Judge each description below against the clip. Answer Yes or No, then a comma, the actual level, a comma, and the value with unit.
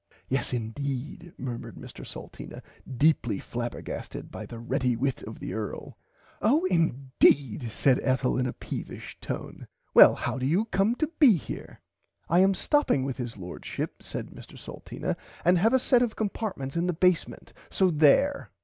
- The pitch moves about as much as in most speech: No, wide, 7.4 semitones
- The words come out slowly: No, average, 160 wpm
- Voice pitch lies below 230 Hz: Yes, medium, 140 Hz